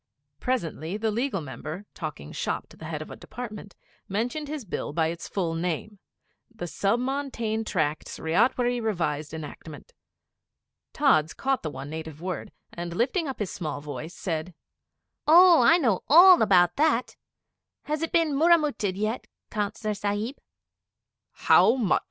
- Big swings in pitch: Yes, wide, 7.8 semitones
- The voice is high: Yes, high, 205 Hz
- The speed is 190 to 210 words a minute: No, average, 145 wpm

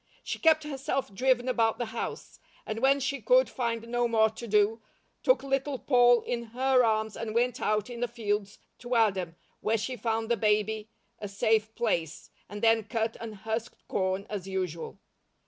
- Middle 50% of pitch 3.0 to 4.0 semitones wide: No, narrow, 2.4 semitones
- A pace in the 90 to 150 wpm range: No, average, 180 wpm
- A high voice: Yes, high, 225 Hz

